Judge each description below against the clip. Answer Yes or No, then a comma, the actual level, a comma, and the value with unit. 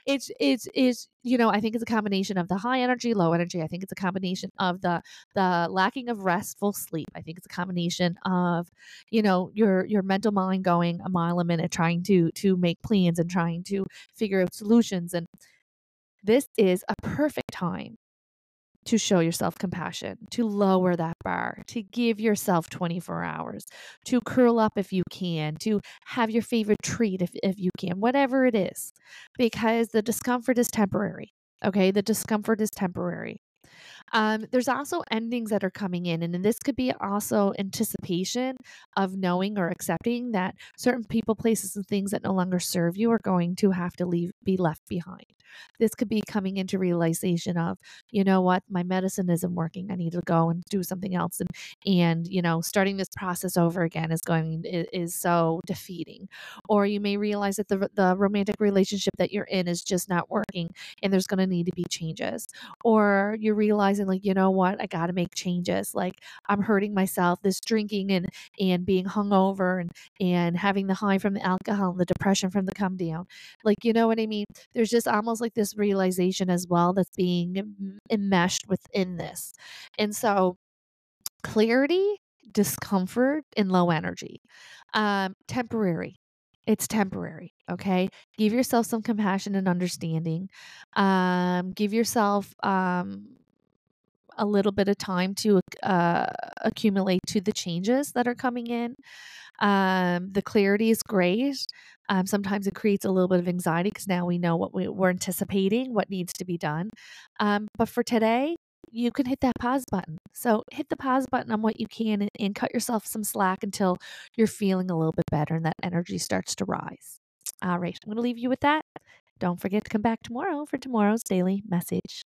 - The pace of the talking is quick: No, average, 185 wpm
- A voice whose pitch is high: Yes, high, 195 Hz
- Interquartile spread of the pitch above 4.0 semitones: No, average, 3.4 semitones